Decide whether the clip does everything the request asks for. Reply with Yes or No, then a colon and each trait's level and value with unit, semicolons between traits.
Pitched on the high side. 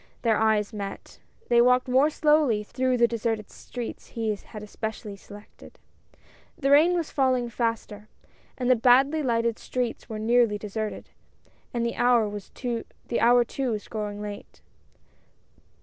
Yes: high, 235 Hz